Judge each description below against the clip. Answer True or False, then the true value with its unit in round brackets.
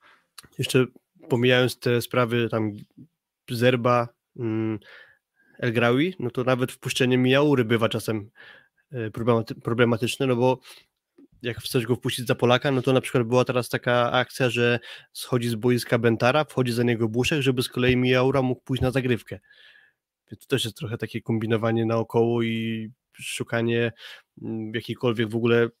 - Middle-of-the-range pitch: False (120 Hz)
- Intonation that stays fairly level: True (1.6 semitones)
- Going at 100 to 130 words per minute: False (145 wpm)